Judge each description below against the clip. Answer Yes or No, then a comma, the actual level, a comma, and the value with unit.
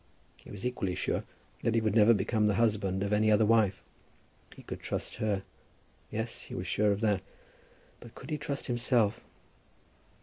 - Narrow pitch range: Yes, narrow, 2.3 semitones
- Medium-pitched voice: No, low, 105 Hz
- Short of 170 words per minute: No, average, 175 wpm